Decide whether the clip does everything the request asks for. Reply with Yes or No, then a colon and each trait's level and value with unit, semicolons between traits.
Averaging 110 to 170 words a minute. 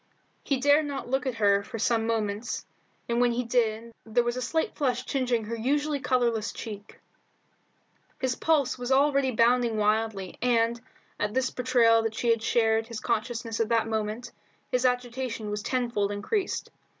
Yes: average, 165 wpm